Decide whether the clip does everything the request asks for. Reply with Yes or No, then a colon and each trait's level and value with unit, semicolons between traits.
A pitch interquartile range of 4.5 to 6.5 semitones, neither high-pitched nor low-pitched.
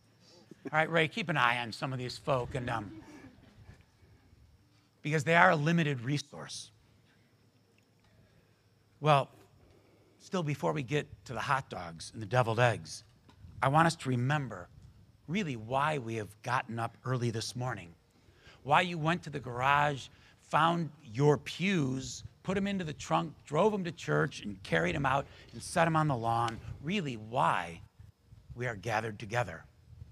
No: average, 5.0 semitones; low, 120 Hz